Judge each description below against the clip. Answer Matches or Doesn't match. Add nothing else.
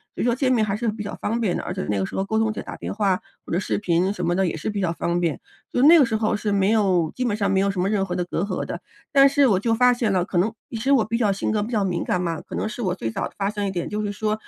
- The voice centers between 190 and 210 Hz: Matches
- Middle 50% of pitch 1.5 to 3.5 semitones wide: Matches